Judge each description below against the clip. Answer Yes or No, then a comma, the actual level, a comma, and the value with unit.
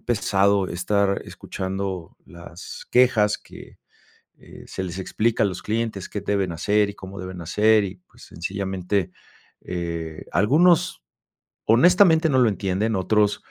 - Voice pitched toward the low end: Yes, low, 100 Hz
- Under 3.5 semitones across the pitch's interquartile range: Yes, average, 2.9 semitones